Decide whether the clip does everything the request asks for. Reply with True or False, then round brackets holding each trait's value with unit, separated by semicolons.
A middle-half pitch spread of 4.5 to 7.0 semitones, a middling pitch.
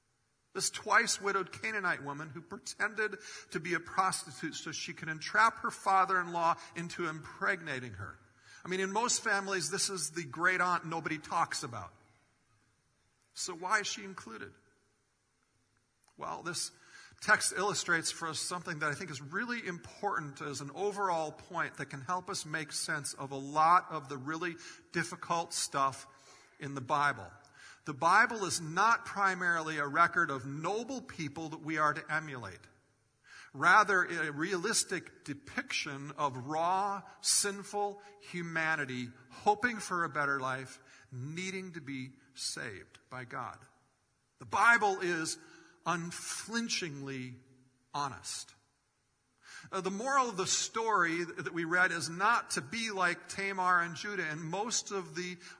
True (5.0 semitones; 170 Hz)